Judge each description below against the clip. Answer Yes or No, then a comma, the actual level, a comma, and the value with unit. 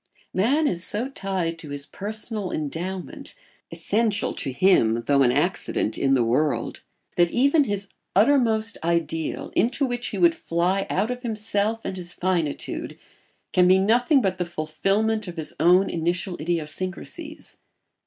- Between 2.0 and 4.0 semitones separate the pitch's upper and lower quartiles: No, average, 5.0 semitones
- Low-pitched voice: No, medium, 185 Hz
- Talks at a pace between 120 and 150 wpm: Yes, average, 145 wpm